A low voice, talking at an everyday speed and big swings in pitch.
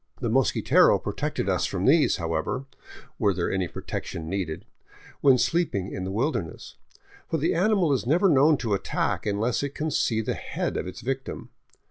Yes: low, 120 Hz; average, 170 wpm; wide, 7.3 semitones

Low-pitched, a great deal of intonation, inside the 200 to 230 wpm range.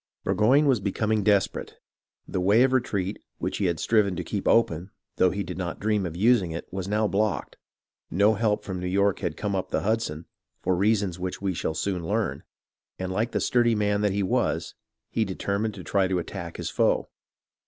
No: low, 100 Hz; average, 2.8 semitones; fast, 205 wpm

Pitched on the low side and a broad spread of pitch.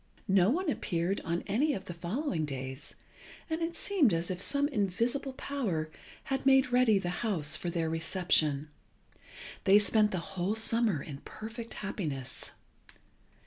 No: high, 195 Hz; wide, 7.1 semitones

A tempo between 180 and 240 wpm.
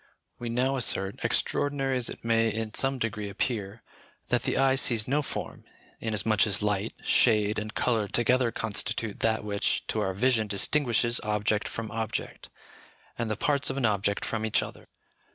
No: average, 170 wpm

